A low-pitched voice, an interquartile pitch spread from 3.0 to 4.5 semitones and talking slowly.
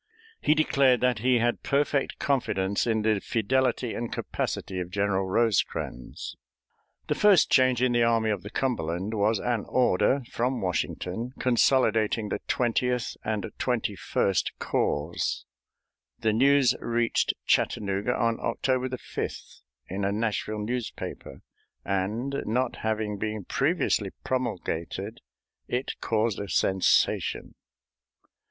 Yes: low, 115 Hz; average, 3.7 semitones; slow, 120 wpm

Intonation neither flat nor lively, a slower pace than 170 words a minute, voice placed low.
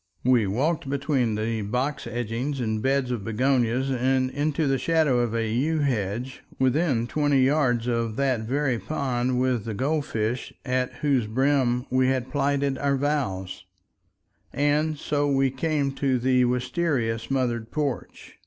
Yes: average, 3.0 semitones; average, 150 wpm; low, 130 Hz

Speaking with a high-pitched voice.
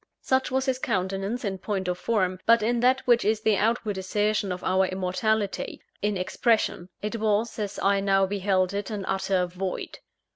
Yes: high, 205 Hz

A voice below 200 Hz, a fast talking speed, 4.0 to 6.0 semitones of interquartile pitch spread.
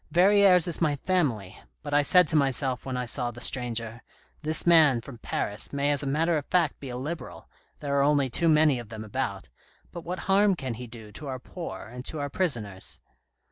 Yes: medium, 140 Hz; fast, 220 wpm; average, 4.9 semitones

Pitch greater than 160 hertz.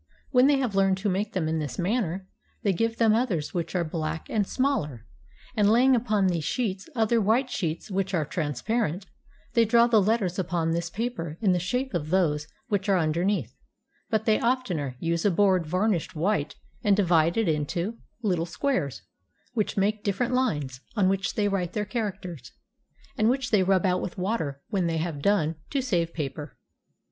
Yes: high, 190 Hz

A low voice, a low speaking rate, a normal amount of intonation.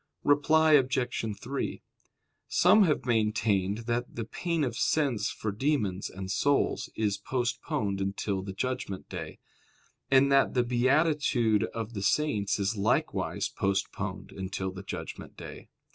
No: low, 115 Hz; slow, 130 wpm; wide, 5.7 semitones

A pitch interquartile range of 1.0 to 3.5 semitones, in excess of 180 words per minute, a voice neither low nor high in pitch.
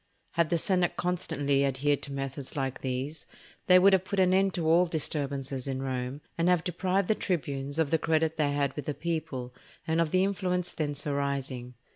No: average, 4.4 semitones; average, 195 wpm; medium, 155 Hz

